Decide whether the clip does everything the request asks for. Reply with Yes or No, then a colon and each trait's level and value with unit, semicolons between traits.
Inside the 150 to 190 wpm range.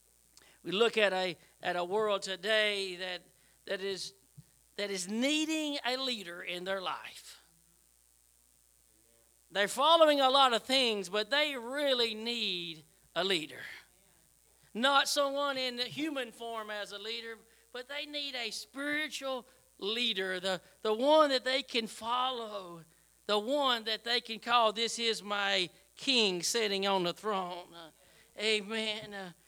No: average, 140 wpm